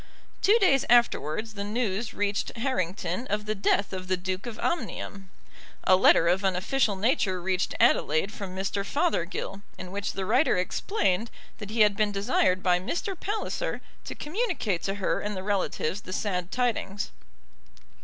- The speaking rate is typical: Yes, average, 165 wpm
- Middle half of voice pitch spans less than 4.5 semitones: Yes, average, 3.7 semitones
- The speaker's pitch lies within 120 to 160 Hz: No, high, 200 Hz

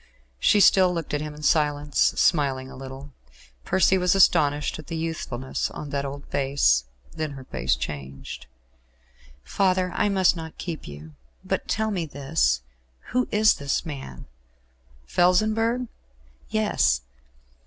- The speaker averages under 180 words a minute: Yes, slow, 135 wpm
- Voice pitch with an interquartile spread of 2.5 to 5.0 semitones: No, wide, 5.4 semitones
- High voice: No, medium, 150 Hz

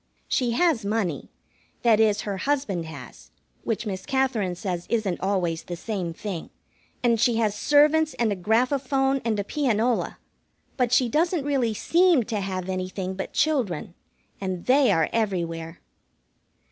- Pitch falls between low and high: No, high, 220 Hz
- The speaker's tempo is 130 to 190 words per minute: Yes, average, 145 wpm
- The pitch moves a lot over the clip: Yes, wide, 5.9 semitones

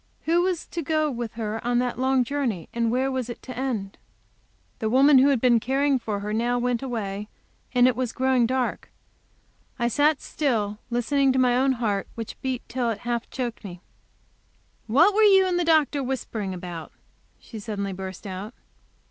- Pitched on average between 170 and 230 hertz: No, high, 245 Hz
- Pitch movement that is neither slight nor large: Yes, average, 3.5 semitones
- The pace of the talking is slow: No, average, 185 wpm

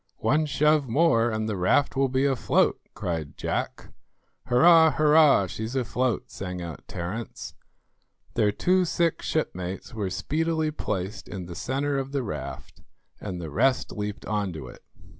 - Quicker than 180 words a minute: No, average, 150 wpm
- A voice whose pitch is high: No, low, 120 Hz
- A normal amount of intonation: No, wide, 7.5 semitones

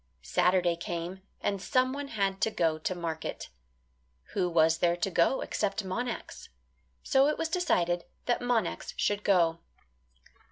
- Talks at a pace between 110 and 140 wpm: Yes, slow, 135 wpm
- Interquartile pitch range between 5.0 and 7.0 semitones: Yes, wide, 5.4 semitones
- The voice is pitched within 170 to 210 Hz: Yes, high, 190 Hz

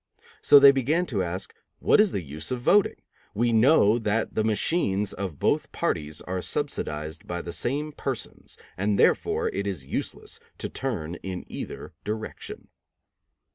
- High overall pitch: No, low, 105 Hz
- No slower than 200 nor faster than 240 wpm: No, average, 155 wpm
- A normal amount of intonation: No, wide, 6.7 semitones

